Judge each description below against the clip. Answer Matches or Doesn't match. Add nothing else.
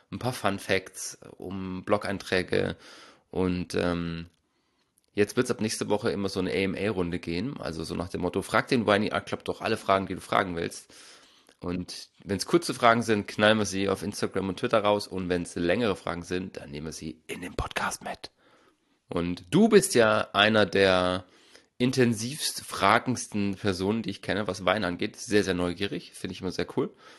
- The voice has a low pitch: Matches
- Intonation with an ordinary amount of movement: Matches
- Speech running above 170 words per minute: Matches